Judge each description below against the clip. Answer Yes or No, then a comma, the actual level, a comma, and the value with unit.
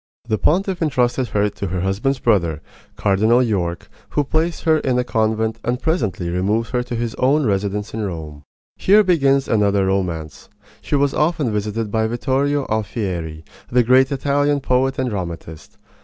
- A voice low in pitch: Yes, low, 115 Hz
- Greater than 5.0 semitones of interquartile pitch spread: Yes, wide, 5.5 semitones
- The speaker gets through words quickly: No, average, 160 wpm